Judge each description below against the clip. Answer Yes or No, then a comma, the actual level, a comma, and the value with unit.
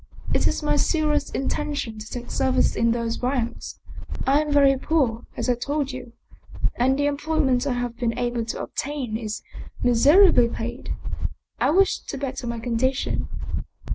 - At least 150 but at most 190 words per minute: Yes, average, 160 wpm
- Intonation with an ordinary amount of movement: Yes, average, 3.4 semitones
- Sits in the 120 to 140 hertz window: No, very high, 255 Hz